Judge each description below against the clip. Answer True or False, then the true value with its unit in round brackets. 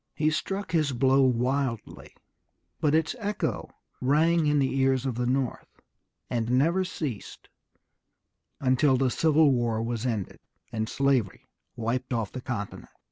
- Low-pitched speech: True (130 Hz)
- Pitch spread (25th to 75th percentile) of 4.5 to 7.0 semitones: False (3.9 semitones)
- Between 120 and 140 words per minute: True (135 wpm)